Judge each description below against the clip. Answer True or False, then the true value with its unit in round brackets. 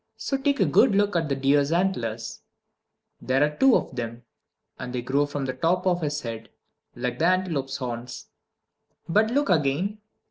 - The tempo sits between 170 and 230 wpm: True (175 wpm)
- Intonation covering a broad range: True (6.4 semitones)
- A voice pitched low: False (145 Hz)